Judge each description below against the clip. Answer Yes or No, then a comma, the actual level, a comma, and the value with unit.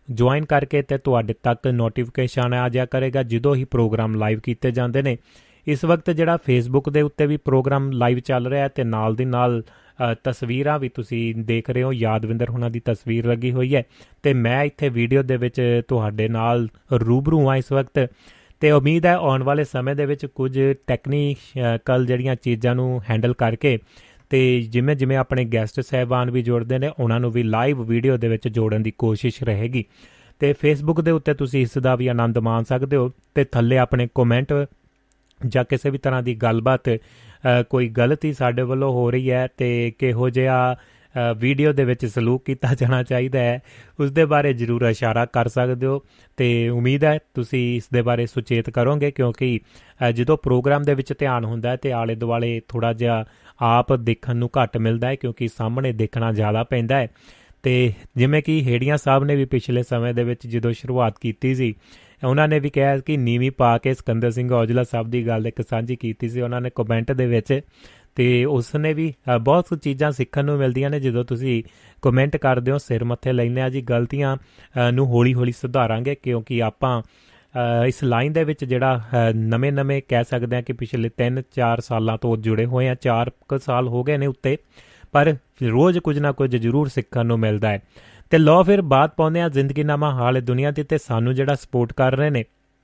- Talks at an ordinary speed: No, fast, 185 wpm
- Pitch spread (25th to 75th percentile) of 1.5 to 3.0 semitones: Yes, narrow, 2.5 semitones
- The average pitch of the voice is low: Yes, low, 125 Hz